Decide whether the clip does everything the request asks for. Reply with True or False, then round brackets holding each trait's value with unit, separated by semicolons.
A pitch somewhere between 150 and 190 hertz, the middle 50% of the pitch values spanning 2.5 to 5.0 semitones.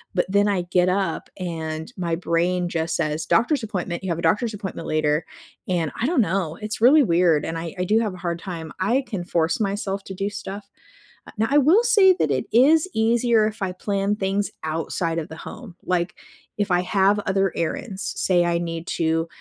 True (185 Hz; 3.9 semitones)